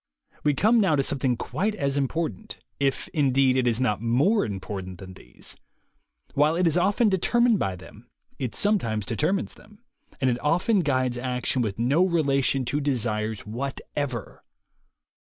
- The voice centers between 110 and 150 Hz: Yes, low, 135 Hz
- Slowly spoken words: No, average, 155 wpm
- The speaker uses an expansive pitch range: Yes, wide, 6.4 semitones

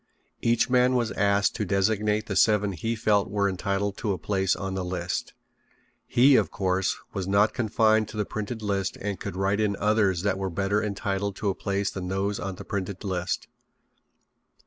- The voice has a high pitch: No, low, 100 Hz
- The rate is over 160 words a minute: Yes, average, 190 wpm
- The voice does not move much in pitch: Yes, narrow, 1.7 semitones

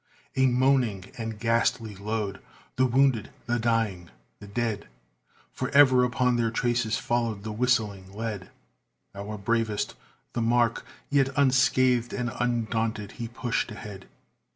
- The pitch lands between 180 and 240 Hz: No, low, 115 Hz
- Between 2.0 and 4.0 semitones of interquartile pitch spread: Yes, narrow, 2.6 semitones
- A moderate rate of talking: No, slow, 130 wpm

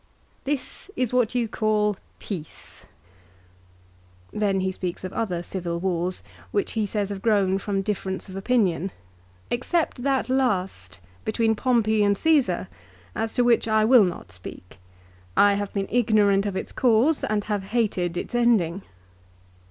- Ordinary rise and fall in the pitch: Yes, average, 3.8 semitones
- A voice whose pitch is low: No, high, 205 Hz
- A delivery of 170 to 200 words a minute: No, average, 150 wpm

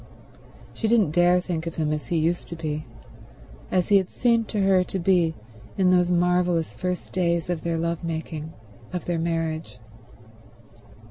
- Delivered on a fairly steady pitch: Yes, narrow, 1.9 semitones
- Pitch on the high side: No, medium, 175 Hz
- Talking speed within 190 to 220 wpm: No, average, 170 wpm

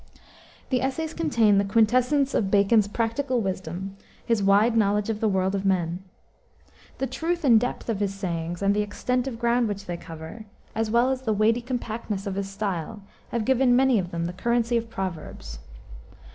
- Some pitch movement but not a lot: Yes, average, 3.7 semitones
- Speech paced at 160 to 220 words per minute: Yes, average, 185 wpm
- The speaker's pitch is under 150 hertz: No, high, 215 Hz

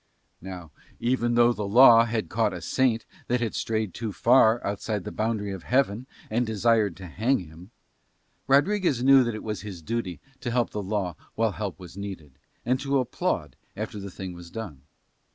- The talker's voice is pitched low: Yes, low, 110 Hz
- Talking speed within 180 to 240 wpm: Yes, average, 185 wpm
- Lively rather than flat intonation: No, average, 3.9 semitones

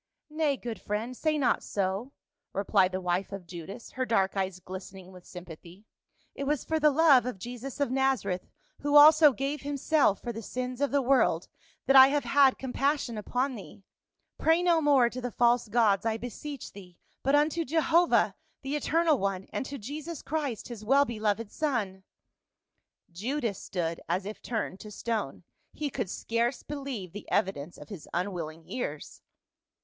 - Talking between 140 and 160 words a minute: No, average, 175 wpm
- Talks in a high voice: Yes, high, 240 Hz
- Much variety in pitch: Yes, wide, 6.4 semitones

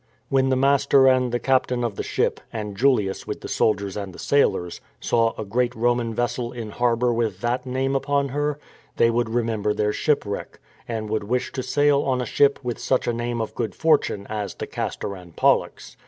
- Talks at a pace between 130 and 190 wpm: No, fast, 205 wpm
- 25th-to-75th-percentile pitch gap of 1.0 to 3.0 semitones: No, average, 3.4 semitones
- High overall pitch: No, low, 120 Hz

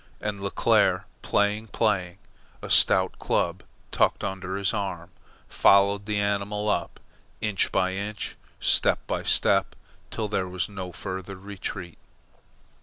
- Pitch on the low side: Yes, low, 100 Hz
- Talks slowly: Yes, slow, 125 wpm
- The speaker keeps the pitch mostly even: Yes, narrow, 1.7 semitones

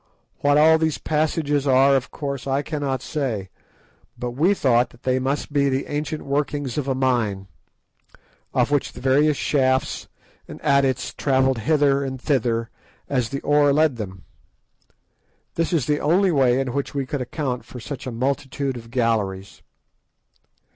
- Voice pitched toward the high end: No, low, 135 Hz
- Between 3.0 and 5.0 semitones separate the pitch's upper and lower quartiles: No, narrow, 2.6 semitones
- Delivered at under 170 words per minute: Yes, average, 160 wpm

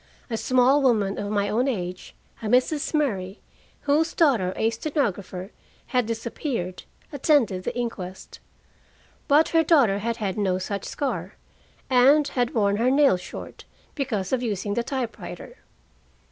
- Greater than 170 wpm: No, average, 140 wpm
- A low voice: No, high, 235 Hz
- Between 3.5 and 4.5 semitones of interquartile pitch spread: No, wide, 5.5 semitones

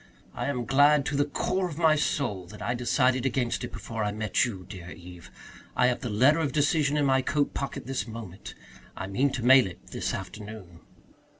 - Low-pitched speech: Yes, low, 125 Hz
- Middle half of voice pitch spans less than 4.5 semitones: No, average, 5.2 semitones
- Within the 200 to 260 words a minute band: Yes, fast, 205 wpm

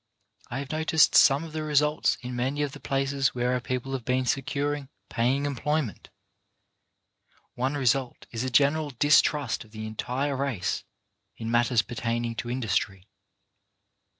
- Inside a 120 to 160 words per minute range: Yes, average, 150 wpm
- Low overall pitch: Yes, low, 130 Hz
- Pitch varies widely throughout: No, average, 3.1 semitones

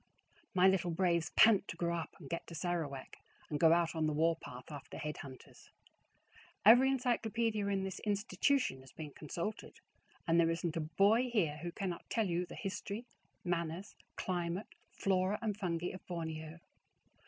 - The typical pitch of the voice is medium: Yes, medium, 175 Hz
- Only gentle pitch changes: No, average, 3.7 semitones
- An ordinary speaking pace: Yes, average, 165 wpm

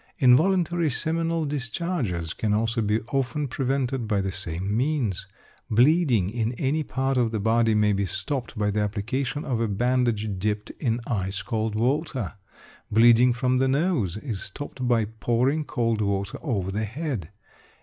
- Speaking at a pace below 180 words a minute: Yes, average, 155 wpm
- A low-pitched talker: Yes, low, 120 Hz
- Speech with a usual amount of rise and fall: Yes, average, 4.4 semitones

